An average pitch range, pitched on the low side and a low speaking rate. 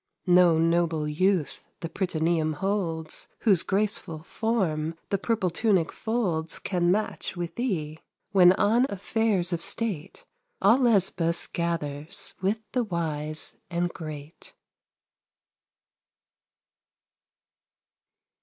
No: average, 3.9 semitones; medium, 175 Hz; slow, 100 wpm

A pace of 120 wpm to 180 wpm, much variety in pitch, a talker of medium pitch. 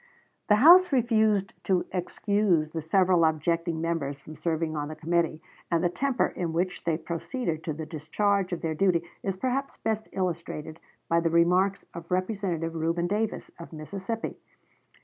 No: average, 160 wpm; average, 3.5 semitones; medium, 170 Hz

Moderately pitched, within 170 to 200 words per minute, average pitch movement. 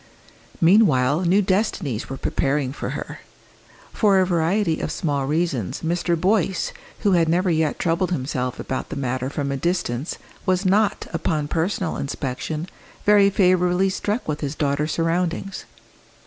No: medium, 165 Hz; average, 145 wpm; average, 4.6 semitones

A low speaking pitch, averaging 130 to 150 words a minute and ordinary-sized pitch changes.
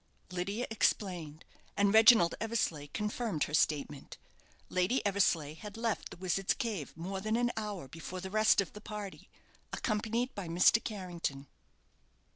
No: high, 195 Hz; average, 140 wpm; average, 4.2 semitones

